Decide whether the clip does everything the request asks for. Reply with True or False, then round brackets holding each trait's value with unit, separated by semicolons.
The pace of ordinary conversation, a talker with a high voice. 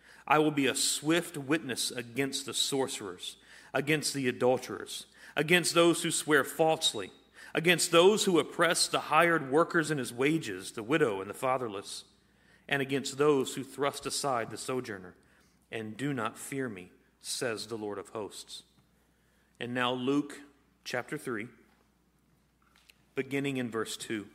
False (145 wpm; 140 Hz)